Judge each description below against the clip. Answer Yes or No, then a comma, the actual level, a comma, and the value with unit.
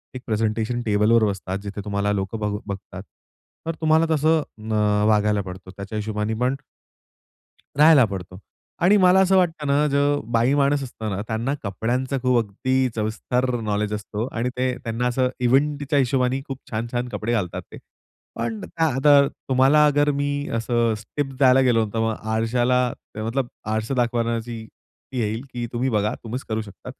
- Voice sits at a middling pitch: No, low, 120 Hz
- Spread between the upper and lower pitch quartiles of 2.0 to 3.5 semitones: No, average, 4.0 semitones